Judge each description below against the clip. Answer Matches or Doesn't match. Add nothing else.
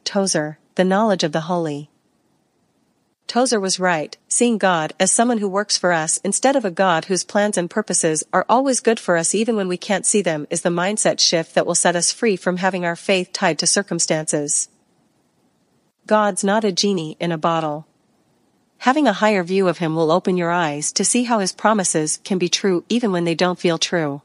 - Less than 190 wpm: Doesn't match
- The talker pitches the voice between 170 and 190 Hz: Matches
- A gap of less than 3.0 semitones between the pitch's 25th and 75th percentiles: Doesn't match